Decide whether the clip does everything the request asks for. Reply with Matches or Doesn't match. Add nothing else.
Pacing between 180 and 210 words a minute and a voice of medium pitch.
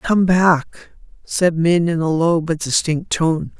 Doesn't match